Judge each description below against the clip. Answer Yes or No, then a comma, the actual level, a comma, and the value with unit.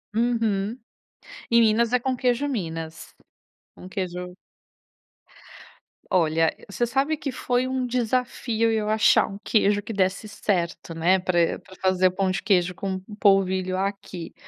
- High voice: Yes, high, 200 Hz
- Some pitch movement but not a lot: Yes, average, 4.0 semitones